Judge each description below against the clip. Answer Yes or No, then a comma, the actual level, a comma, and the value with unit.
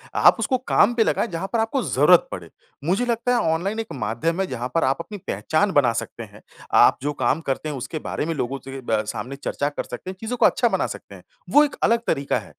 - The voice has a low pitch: No, medium, 160 Hz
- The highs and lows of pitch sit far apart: Yes, wide, 8.5 semitones